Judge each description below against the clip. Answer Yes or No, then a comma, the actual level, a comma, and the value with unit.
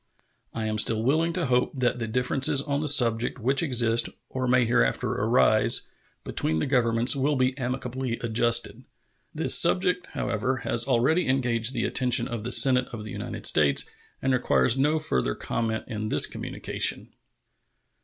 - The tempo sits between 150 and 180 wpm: Yes, average, 160 wpm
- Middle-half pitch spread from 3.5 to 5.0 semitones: No, average, 2.7 semitones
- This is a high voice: No, low, 125 Hz